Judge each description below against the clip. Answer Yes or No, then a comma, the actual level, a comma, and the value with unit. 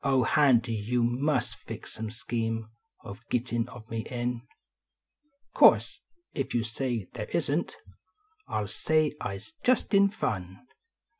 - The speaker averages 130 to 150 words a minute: Yes, average, 145 wpm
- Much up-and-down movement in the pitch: No, average, 3.2 semitones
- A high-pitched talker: No, low, 120 Hz